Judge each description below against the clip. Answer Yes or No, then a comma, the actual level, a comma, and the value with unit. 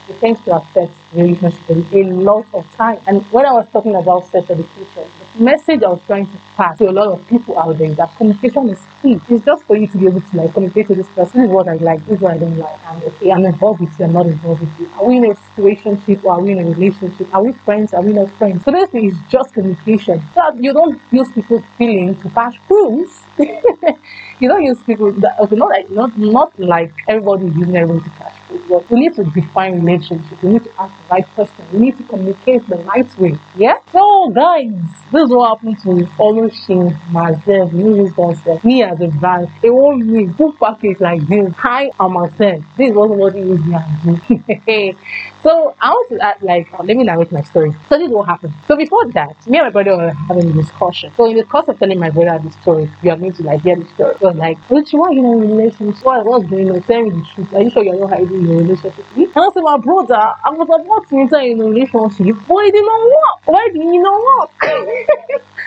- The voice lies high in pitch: Yes, high, 200 Hz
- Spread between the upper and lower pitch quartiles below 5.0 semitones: No, wide, 5.4 semitones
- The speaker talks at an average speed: No, fast, 245 wpm